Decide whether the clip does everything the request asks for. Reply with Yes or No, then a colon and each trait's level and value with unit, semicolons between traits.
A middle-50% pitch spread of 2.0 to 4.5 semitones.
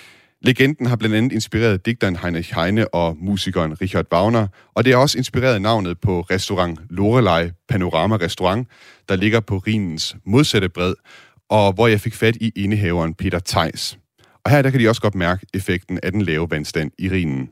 Yes: average, 4.2 semitones